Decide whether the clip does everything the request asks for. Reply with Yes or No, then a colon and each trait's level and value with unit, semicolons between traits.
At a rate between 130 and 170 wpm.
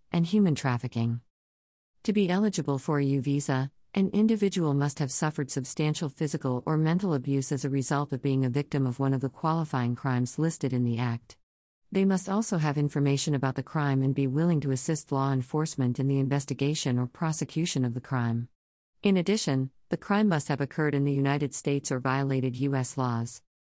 No: average, 190 wpm